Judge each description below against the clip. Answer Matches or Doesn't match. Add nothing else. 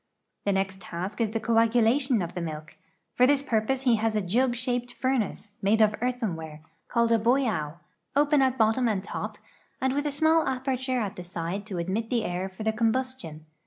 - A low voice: Doesn't match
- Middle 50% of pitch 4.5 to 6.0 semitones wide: Matches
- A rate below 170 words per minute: Doesn't match